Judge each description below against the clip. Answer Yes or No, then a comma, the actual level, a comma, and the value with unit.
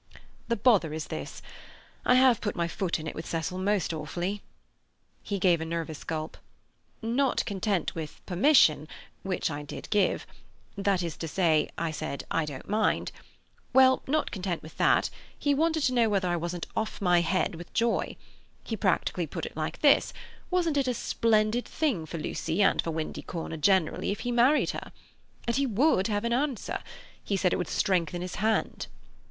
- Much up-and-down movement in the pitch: Yes, wide, 6.0 semitones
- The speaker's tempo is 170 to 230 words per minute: Yes, average, 175 wpm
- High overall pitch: Yes, high, 195 Hz